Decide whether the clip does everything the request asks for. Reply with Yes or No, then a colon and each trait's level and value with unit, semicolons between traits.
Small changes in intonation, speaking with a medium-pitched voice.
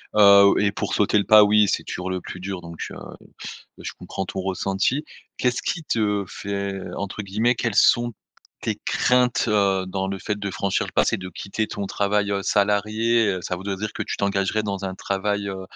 No: narrow, 1.7 semitones; low, 100 Hz